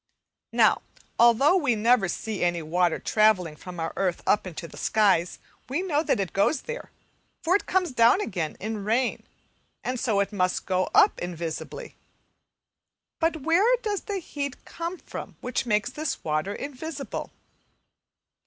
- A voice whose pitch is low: No, high, 225 Hz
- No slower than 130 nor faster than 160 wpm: Yes, average, 155 wpm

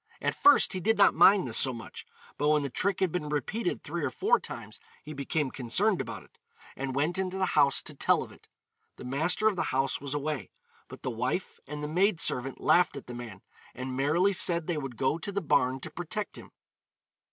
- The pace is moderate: No, fast, 220 wpm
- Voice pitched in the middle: Yes, medium, 150 Hz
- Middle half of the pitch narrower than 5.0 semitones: No, average, 5.3 semitones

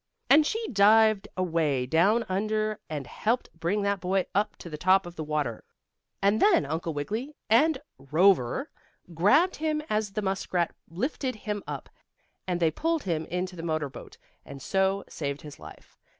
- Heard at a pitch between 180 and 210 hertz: Yes, high, 190 Hz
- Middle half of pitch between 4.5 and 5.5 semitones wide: Yes, average, 4.9 semitones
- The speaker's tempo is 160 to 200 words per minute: Yes, average, 165 wpm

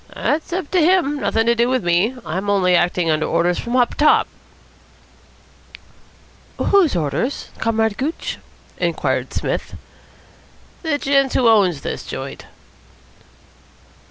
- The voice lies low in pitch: No, high, 235 Hz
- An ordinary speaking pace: No, slow, 125 wpm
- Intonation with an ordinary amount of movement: No, wide, 8.1 semitones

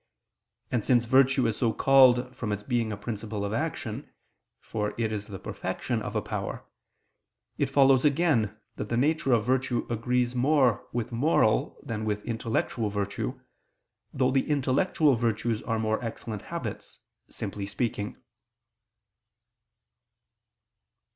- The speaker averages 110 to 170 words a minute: Yes, slow, 135 wpm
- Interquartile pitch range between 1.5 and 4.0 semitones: Yes, average, 3.4 semitones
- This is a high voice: No, low, 115 Hz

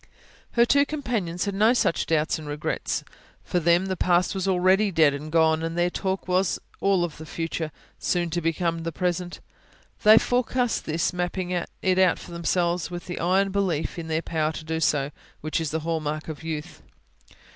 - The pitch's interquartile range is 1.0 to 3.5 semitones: Yes, average, 2.8 semitones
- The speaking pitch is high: No, medium, 175 Hz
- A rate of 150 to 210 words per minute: Yes, average, 190 wpm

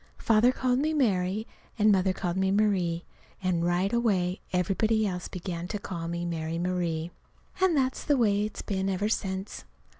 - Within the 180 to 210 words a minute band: No, average, 170 wpm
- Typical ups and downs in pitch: Yes, average, 3.4 semitones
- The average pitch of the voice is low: No, high, 190 Hz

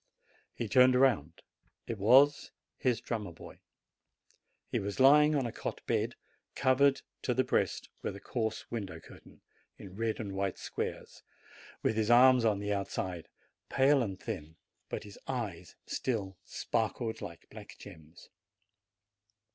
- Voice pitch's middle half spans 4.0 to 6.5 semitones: Yes, average, 4.7 semitones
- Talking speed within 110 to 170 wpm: Yes, average, 140 wpm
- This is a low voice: Yes, low, 110 Hz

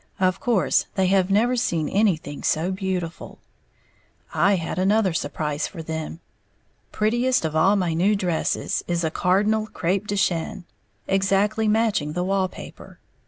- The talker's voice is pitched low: No, high, 190 Hz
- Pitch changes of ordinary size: Yes, average, 3.8 semitones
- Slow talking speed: No, average, 145 wpm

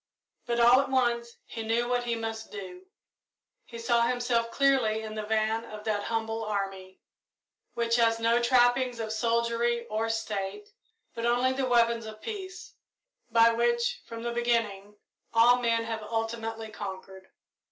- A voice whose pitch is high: Yes, high, 230 Hz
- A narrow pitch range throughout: Yes, narrow, 1.4 semitones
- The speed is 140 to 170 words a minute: Yes, average, 150 wpm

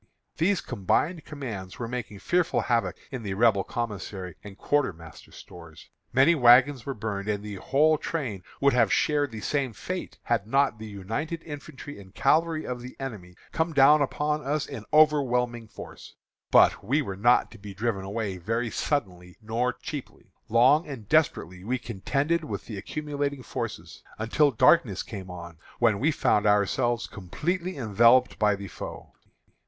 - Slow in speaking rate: No, average, 160 wpm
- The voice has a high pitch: No, low, 120 Hz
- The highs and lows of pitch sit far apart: Yes, wide, 6.0 semitones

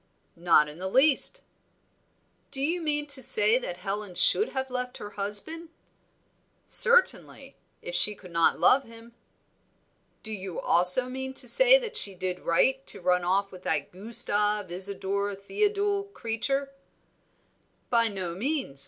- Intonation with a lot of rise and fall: Yes, wide, 6.6 semitones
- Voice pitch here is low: No, high, 225 Hz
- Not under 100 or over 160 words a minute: Yes, average, 145 wpm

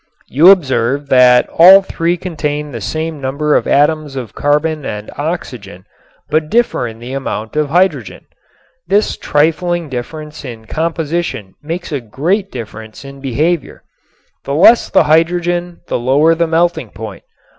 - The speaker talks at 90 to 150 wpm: Yes, average, 145 wpm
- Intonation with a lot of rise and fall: No, average, 4.8 semitones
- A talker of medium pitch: Yes, medium, 150 Hz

